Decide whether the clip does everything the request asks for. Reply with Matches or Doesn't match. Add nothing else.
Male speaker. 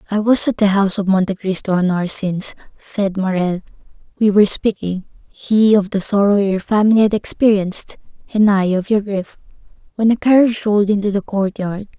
Doesn't match